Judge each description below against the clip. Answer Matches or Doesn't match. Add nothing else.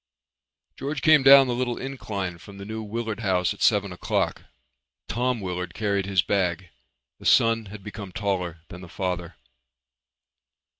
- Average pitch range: Matches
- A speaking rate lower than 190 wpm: Matches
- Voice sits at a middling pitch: Doesn't match